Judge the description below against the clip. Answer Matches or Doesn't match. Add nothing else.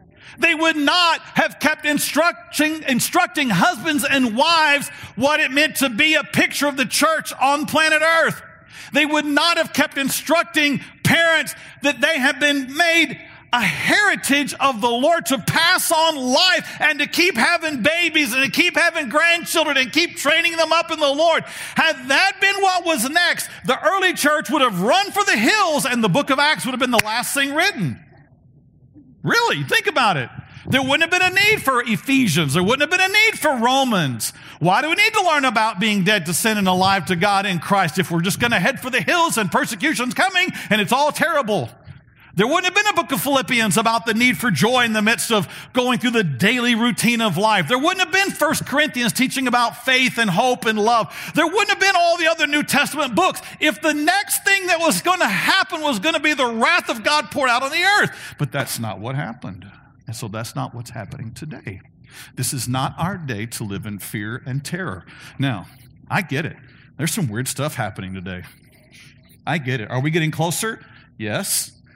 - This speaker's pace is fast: Matches